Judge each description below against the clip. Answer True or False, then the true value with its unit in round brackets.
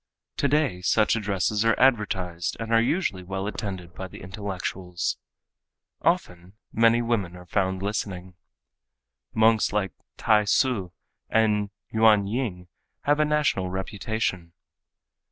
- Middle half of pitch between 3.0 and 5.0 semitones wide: True (3.5 semitones)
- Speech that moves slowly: True (120 wpm)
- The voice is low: True (100 Hz)